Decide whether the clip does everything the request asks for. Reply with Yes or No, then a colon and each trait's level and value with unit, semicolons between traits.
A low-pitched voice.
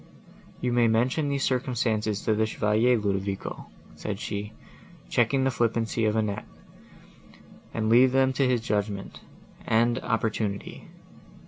Yes: low, 115 Hz